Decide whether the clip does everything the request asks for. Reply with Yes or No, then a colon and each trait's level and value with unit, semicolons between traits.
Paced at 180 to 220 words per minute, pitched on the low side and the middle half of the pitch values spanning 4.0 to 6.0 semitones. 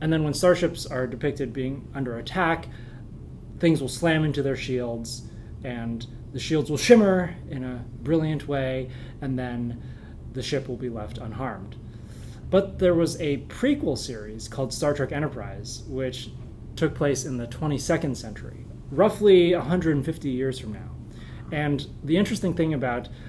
No: average, 150 wpm; low, 130 Hz; average, 4.6 semitones